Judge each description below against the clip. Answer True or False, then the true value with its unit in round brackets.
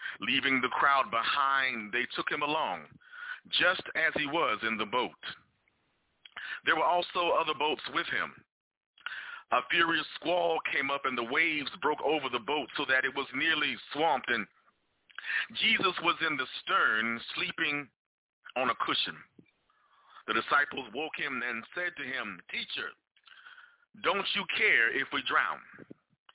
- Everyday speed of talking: True (150 wpm)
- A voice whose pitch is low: False (165 Hz)